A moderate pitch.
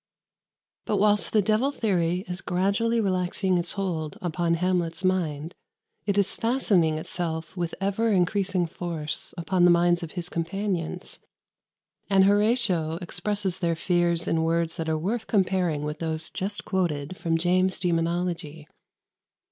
Yes: medium, 180 Hz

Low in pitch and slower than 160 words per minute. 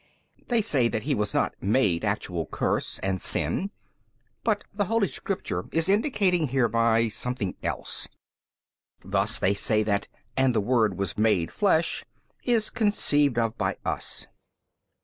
Yes: low, 125 Hz; average, 140 wpm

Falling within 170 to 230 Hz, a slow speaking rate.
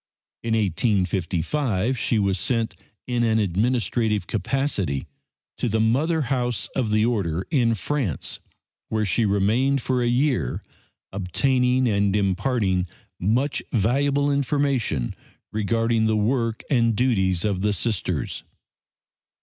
No: low, 115 Hz; slow, 115 wpm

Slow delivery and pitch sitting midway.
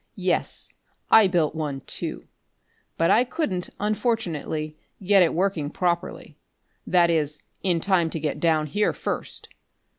Yes: slow, 130 wpm; medium, 170 Hz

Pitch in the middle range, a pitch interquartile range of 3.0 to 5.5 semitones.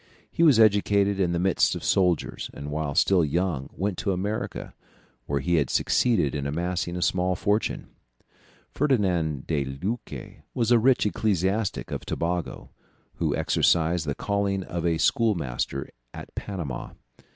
No: very low, 90 Hz; average, 4.5 semitones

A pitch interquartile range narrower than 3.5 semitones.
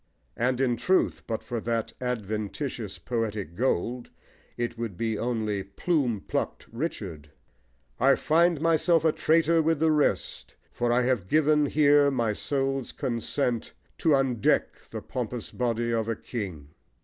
No: average, 4.6 semitones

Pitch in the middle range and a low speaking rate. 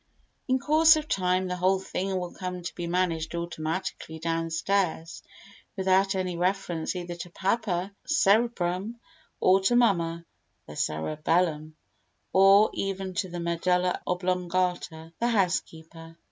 Yes: medium, 180 Hz; slow, 130 wpm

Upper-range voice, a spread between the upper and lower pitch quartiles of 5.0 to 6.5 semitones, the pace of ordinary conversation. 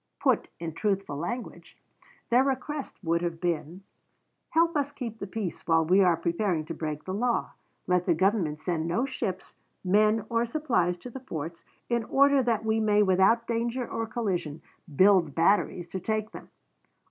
Yes: high, 195 Hz; wide, 5.5 semitones; average, 170 wpm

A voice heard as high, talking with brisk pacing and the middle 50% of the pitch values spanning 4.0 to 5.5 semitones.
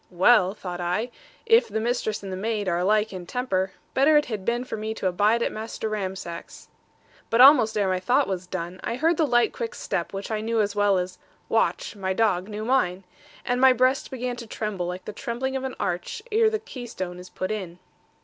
Yes: high, 215 Hz; fast, 215 wpm; average, 4.7 semitones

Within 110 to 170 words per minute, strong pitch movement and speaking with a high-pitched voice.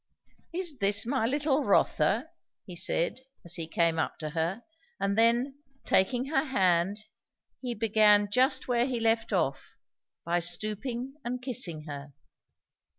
Yes: average, 140 wpm; wide, 6.4 semitones; high, 215 Hz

